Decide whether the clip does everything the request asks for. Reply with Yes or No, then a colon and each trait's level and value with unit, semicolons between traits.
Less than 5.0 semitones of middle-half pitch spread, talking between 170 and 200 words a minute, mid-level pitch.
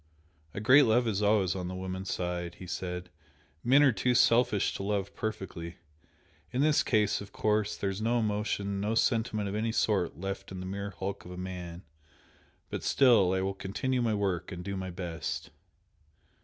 No: average, 2.9 semitones; average, 180 wpm; low, 100 Hz